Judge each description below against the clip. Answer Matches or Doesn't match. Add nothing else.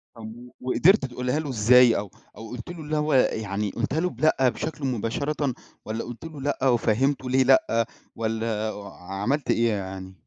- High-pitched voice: Doesn't match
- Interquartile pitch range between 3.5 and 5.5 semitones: Matches